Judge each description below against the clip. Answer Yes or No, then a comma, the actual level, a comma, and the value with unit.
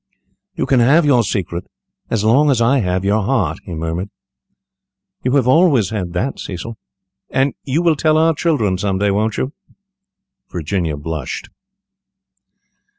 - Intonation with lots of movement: Yes, wide, 7.0 semitones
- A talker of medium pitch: No, low, 110 Hz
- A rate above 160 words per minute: No, average, 150 wpm